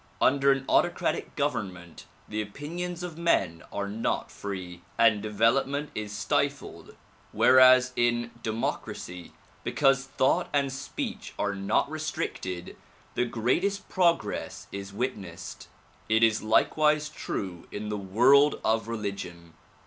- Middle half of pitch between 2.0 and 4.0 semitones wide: No, wide, 5.6 semitones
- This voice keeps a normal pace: No, slow, 120 wpm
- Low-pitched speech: Yes, low, 115 Hz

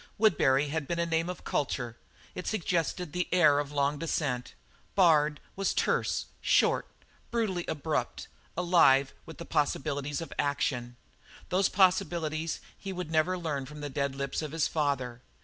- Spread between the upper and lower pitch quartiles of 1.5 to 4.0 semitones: Yes, average, 3.7 semitones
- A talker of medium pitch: Yes, medium, 155 Hz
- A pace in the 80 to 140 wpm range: No, average, 150 wpm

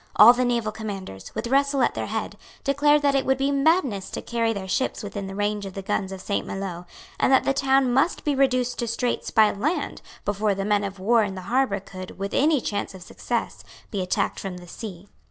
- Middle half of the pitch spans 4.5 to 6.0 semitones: Yes, average, 5.3 semitones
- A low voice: No, high, 220 Hz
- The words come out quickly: Yes, fast, 225 wpm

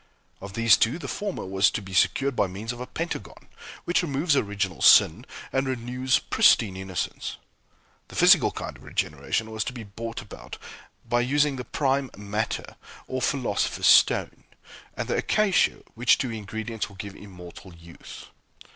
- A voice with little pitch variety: No, average, 4.8 semitones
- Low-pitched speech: Yes, low, 115 Hz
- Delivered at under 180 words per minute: Yes, average, 160 wpm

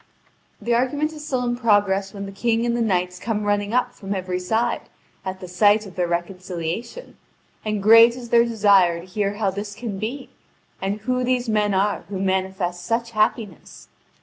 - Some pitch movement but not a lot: Yes, average, 3.7 semitones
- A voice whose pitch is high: Yes, high, 205 Hz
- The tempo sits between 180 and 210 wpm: Yes, average, 185 wpm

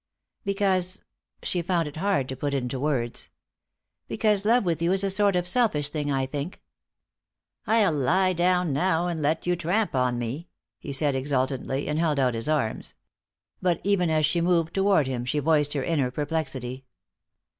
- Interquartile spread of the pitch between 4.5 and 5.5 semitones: Yes, average, 4.9 semitones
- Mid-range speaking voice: Yes, medium, 155 Hz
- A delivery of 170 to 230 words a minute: Yes, average, 175 wpm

